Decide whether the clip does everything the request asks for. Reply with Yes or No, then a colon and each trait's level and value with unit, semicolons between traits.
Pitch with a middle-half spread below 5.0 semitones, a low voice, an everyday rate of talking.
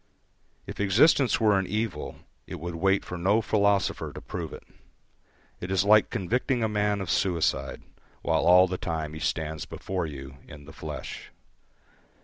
Yes: average, 4.0 semitones; very low, 95 Hz; average, 160 wpm